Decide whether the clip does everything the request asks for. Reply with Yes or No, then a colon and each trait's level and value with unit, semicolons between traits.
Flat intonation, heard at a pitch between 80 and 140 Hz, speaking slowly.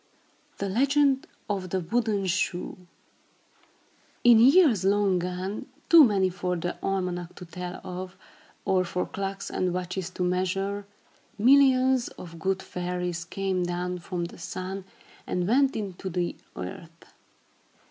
No: narrow, 2.3 semitones; medium, 185 Hz; slow, 130 wpm